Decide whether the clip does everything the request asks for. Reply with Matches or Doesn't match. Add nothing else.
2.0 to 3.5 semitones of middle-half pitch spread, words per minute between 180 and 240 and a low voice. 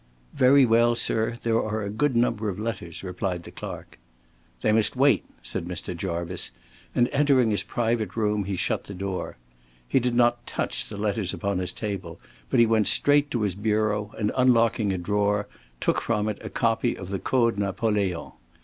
Matches